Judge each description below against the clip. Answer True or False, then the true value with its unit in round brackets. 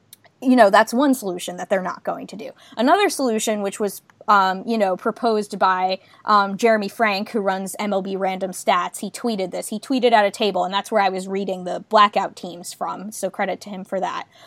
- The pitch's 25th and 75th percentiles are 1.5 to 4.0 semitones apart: True (2.8 semitones)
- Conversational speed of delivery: False (215 wpm)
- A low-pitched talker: False (200 Hz)